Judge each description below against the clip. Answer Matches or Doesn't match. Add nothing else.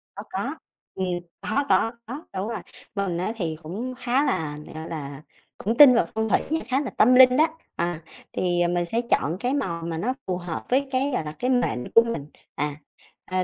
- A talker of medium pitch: Doesn't match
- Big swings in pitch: Matches